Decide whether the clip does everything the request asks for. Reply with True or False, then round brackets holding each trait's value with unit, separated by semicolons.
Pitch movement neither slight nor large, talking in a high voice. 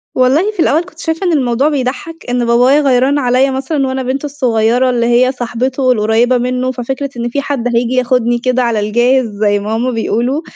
False (2.3 semitones; 255 Hz)